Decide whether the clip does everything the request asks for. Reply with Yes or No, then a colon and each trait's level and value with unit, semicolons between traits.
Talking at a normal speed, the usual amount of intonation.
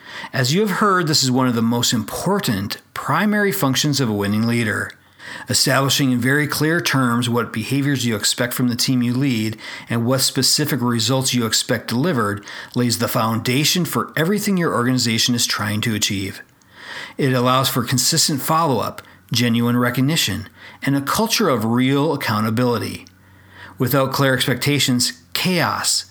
Yes: average, 155 wpm; average, 3.3 semitones